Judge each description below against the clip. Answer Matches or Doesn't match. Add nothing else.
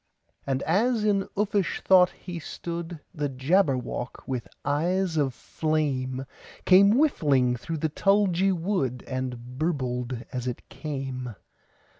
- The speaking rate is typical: Doesn't match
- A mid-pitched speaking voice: Matches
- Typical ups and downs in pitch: Doesn't match